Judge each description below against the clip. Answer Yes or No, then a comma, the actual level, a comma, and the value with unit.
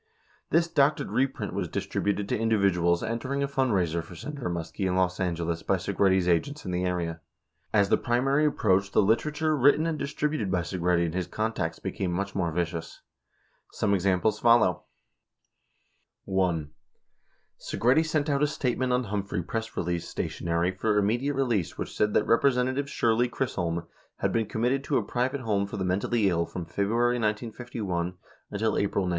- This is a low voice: Yes, low, 105 Hz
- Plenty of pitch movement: Yes, wide, 5.7 semitones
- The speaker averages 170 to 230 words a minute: Yes, average, 175 wpm